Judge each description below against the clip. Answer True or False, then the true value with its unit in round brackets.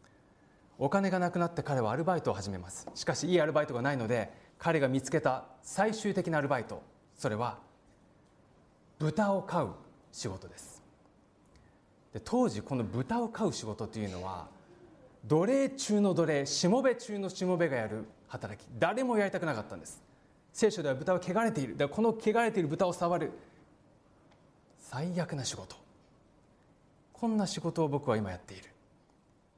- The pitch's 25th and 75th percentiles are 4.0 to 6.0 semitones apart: False (8.1 semitones)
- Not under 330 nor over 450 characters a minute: False (315 characters per minute)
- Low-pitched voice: False (160 Hz)